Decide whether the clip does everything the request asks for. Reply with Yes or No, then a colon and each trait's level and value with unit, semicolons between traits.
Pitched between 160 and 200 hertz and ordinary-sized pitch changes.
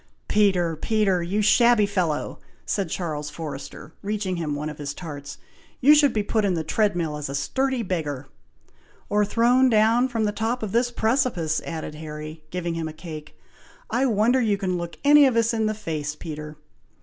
No: high, 190 Hz; wide, 6.3 semitones